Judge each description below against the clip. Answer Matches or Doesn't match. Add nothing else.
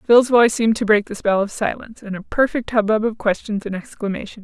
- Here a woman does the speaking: Matches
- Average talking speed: Doesn't match